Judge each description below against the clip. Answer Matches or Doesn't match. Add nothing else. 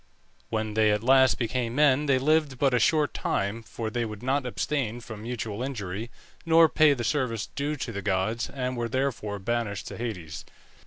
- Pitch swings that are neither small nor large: Matches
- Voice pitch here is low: Matches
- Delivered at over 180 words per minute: Matches